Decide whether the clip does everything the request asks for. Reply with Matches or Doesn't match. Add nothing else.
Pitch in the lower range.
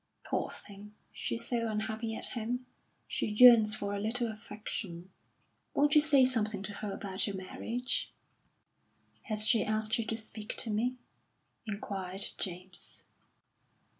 Doesn't match